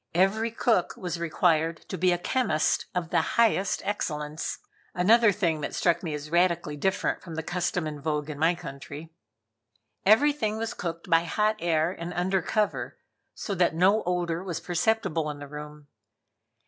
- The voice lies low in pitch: No, medium, 175 Hz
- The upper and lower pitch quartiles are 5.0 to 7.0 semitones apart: No, average, 3.5 semitones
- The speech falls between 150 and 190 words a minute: Yes, average, 165 wpm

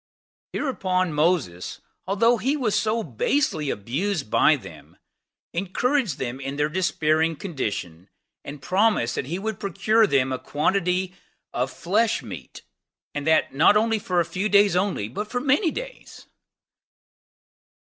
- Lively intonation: Yes, wide, 6.7 semitones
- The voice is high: No, medium, 180 Hz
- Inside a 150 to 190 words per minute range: No, slow, 135 wpm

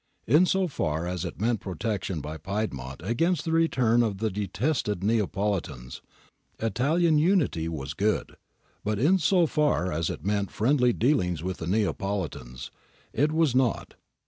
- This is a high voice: No, low, 105 Hz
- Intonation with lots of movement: Yes, wide, 8.0 semitones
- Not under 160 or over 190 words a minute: No, average, 150 wpm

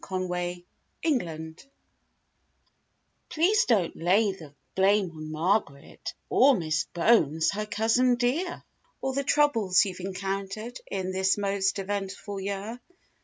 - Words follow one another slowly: Yes, slow, 120 wpm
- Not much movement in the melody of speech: No, average, 4.2 semitones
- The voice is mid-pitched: No, high, 195 Hz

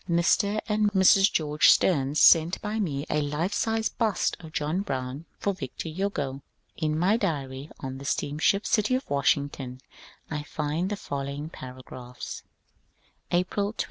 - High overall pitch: No, medium, 155 Hz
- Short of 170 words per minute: Yes, average, 150 wpm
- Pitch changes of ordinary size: No, wide, 5.9 semitones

